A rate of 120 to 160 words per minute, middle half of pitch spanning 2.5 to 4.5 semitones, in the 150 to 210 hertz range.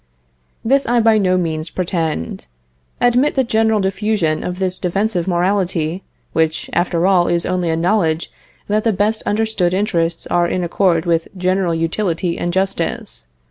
Yes: average, 150 wpm; average, 3.6 semitones; medium, 185 Hz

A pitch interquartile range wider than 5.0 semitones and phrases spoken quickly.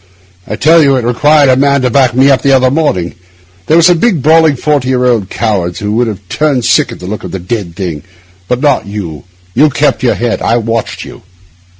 Yes: wide, 5.5 semitones; fast, 230 wpm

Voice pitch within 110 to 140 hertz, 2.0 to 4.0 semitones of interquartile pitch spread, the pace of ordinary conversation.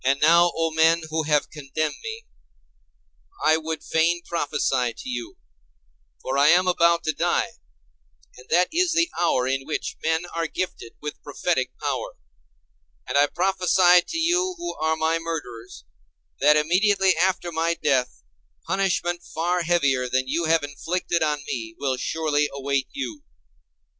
No: medium, 160 Hz; average, 3.7 semitones; average, 150 wpm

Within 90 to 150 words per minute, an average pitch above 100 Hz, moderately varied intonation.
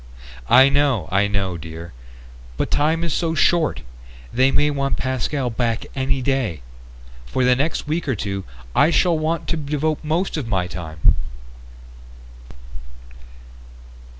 No: slow, 135 wpm; low, 135 Hz; wide, 6.9 semitones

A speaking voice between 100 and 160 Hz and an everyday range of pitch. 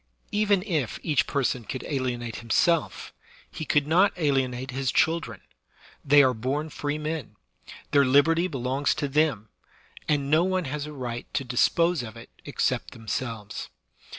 Yes: medium, 140 Hz; average, 3.9 semitones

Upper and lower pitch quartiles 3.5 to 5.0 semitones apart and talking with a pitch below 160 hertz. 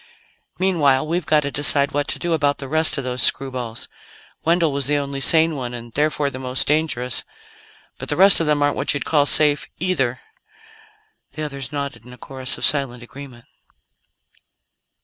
No: average, 2.9 semitones; medium, 140 Hz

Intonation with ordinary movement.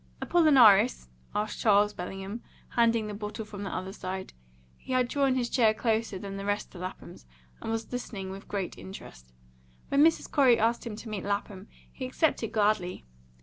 Yes: average, 3.4 semitones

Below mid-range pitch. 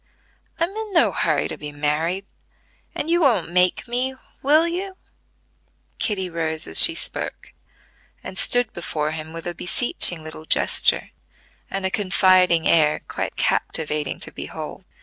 No: medium, 180 Hz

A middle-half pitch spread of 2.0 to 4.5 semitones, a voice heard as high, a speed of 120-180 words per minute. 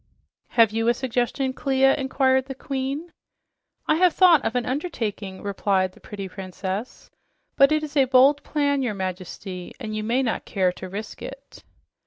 No: wide, 5.4 semitones; very high, 250 Hz; average, 170 wpm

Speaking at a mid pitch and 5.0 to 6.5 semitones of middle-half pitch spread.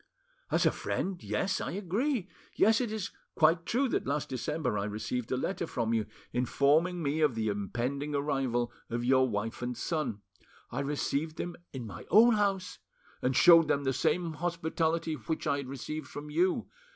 Yes: medium, 150 Hz; wide, 5.5 semitones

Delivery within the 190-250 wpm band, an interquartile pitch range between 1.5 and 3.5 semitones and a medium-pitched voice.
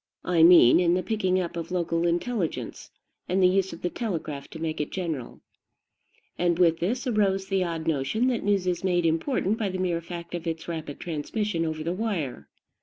Yes: average, 195 wpm; average, 2.7 semitones; medium, 175 Hz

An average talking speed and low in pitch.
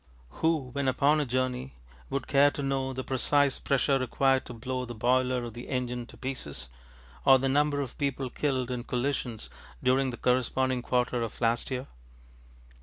Yes: average, 175 wpm; low, 130 Hz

